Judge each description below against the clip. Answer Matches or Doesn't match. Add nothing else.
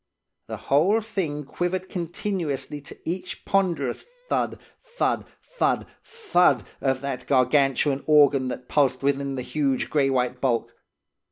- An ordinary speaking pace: Doesn't match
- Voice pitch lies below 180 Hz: Matches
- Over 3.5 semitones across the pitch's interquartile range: Matches